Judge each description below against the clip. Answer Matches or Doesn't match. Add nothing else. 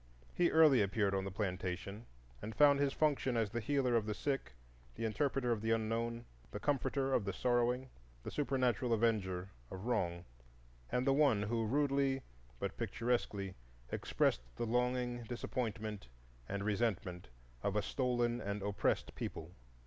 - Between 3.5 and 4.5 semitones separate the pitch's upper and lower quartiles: Matches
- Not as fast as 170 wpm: Matches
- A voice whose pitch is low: Matches